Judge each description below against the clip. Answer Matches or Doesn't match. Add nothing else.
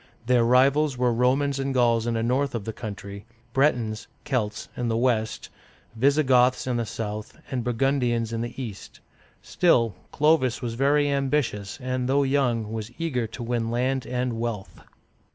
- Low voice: Matches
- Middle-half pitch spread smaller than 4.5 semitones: Matches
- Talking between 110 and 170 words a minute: Matches